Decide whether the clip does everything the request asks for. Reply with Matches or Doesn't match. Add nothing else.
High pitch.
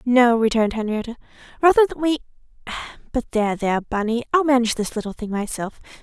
Matches